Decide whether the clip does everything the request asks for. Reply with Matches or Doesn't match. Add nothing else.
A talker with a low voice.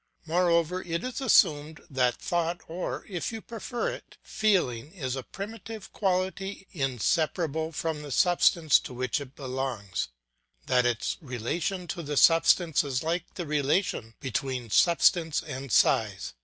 Doesn't match